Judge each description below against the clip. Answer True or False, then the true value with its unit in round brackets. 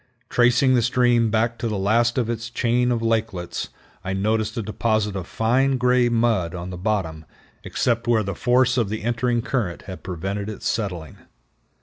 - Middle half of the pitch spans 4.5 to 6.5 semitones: False (3.3 semitones)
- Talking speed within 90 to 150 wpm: False (180 wpm)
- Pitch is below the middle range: True (115 Hz)